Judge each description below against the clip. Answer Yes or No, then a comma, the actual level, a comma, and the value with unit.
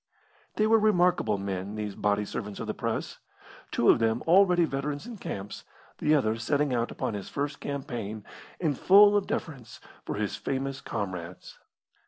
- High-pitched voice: No, low, 135 Hz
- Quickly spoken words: No, average, 165 wpm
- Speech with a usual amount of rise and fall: No, wide, 8.3 semitones